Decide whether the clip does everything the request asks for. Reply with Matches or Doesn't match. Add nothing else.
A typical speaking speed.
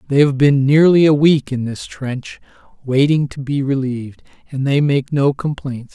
Matches